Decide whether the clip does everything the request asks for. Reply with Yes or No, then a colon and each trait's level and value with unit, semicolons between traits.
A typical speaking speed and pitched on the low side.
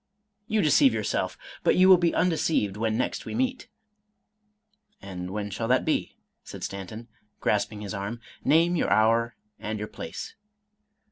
Yes: average, 165 wpm; low, 115 Hz